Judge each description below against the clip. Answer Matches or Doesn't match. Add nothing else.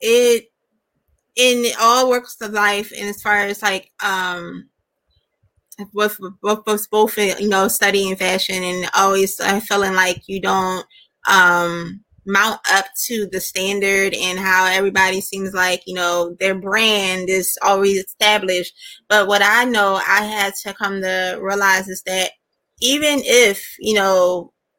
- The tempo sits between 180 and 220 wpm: Doesn't match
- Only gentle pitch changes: Matches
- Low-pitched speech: Doesn't match